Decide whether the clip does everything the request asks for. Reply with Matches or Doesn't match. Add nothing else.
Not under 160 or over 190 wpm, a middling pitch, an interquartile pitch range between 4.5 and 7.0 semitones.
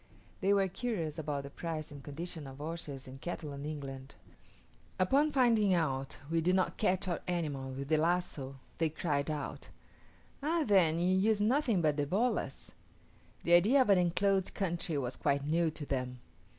Matches